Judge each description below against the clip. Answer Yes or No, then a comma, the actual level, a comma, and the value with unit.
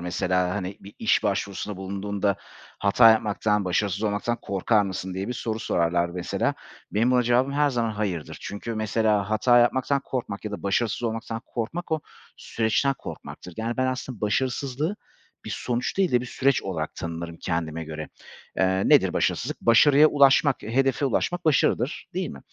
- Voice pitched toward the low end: Yes, low, 110 Hz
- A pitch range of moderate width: Yes, average, 4.6 semitones